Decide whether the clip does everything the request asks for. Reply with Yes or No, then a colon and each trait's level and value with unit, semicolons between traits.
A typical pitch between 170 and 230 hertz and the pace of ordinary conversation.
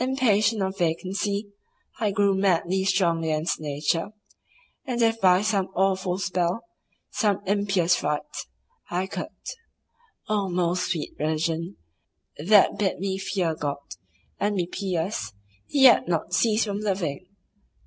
No: high, 190 Hz; slow, 125 wpm